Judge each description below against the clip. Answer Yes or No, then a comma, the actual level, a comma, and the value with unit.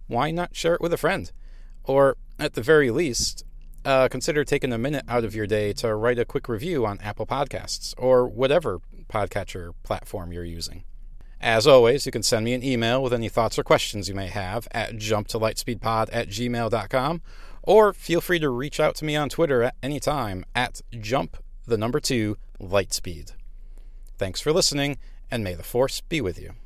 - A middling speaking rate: Yes, average, 180 wpm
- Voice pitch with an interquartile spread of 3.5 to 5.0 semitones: No, wide, 5.4 semitones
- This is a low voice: Yes, low, 115 Hz